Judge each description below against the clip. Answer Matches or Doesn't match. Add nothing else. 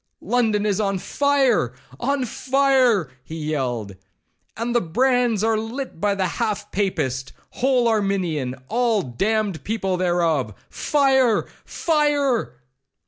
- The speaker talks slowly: Matches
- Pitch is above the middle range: Matches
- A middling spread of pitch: Doesn't match